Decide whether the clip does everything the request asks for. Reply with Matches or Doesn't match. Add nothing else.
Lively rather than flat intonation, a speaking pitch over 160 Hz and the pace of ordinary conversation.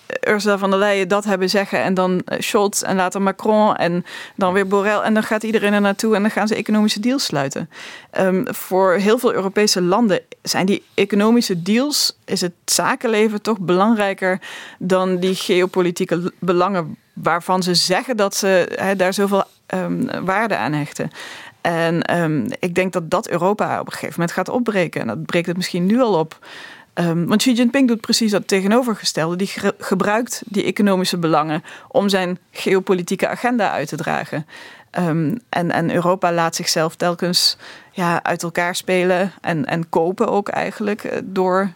Doesn't match